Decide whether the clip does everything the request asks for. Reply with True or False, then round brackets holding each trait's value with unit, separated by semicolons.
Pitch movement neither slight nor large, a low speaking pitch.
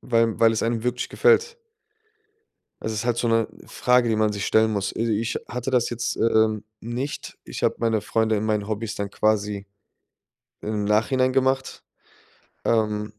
False (2.2 semitones; 110 Hz)